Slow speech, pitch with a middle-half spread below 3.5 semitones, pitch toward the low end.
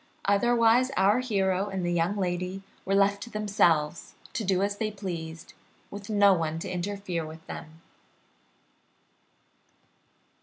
No: slow, 130 wpm; average, 2.8 semitones; high, 195 Hz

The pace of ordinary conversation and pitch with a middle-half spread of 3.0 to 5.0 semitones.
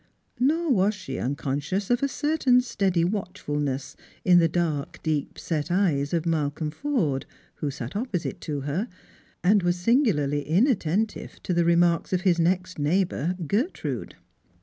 No: average, 145 wpm; wide, 5.5 semitones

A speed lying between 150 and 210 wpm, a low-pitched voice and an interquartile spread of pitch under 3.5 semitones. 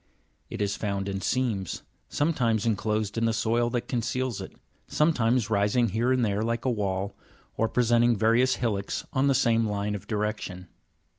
Yes: average, 165 wpm; low, 115 Hz; average, 2.8 semitones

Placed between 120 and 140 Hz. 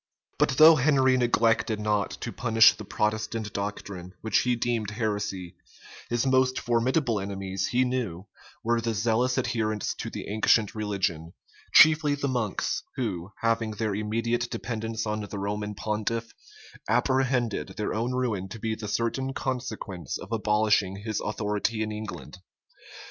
No: low, 110 Hz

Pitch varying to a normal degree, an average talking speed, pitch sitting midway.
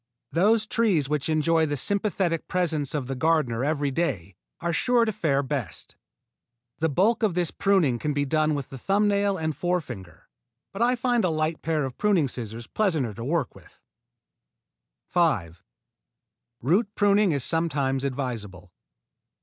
No: wide, 6.1 semitones; average, 155 wpm; medium, 155 Hz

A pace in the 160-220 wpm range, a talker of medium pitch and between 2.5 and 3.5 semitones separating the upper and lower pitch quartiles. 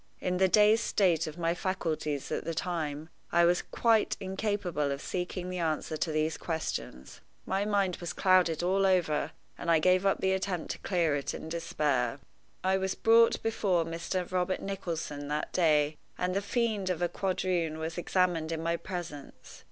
Yes: average, 175 wpm; medium, 175 Hz; average, 3.0 semitones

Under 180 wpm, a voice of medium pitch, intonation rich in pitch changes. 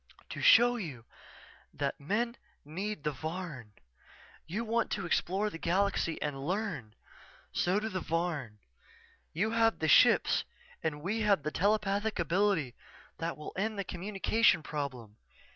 Yes: average, 140 wpm; medium, 180 Hz; wide, 5.7 semitones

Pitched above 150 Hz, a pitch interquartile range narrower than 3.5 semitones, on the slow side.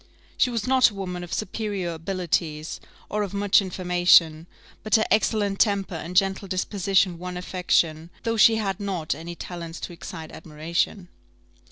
No: medium, 185 Hz; average, 3.1 semitones; average, 155 wpm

